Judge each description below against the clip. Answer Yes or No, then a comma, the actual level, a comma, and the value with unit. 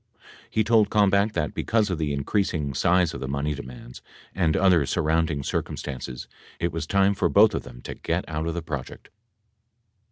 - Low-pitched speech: Yes, very low, 80 Hz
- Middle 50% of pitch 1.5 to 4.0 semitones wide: No, wide, 5.4 semitones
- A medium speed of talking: Yes, average, 180 wpm